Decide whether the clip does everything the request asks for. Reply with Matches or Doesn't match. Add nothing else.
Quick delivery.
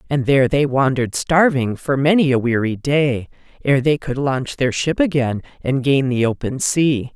Doesn't match